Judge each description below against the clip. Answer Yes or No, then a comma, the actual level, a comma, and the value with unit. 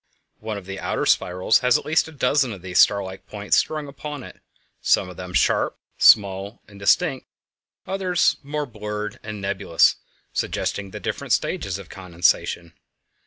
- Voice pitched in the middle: No, low, 105 Hz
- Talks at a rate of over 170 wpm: No, average, 160 wpm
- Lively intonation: Yes, wide, 6.4 semitones